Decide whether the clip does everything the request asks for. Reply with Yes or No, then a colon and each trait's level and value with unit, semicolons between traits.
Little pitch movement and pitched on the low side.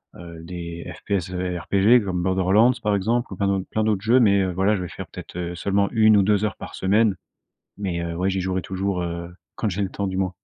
Yes: narrow, 2.3 semitones; very low, 95 Hz